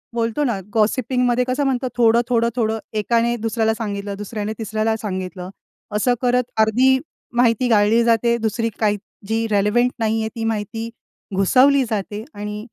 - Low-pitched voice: No, high, 225 Hz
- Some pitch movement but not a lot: No, narrow, 2.2 semitones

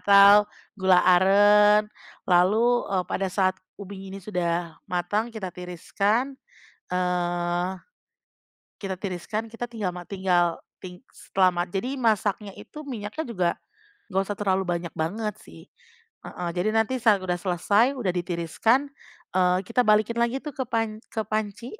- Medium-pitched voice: No, high, 195 Hz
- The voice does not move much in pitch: No, average, 3.5 semitones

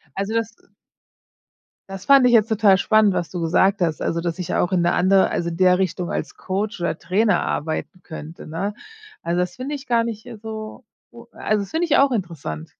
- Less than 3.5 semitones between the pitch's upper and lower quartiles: No, average, 4.2 semitones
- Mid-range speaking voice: No, high, 195 Hz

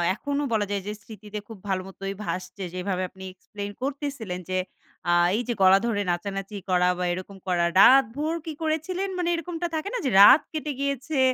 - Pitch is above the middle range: Yes, high, 215 Hz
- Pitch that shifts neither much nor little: No, wide, 7.1 semitones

